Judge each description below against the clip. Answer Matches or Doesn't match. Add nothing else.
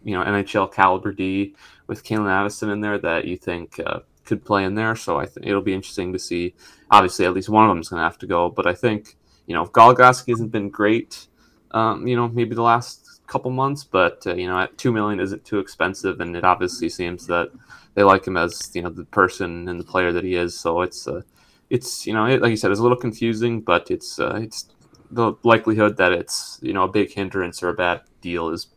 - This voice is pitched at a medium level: Doesn't match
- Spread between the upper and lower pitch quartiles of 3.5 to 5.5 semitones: Matches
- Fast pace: Matches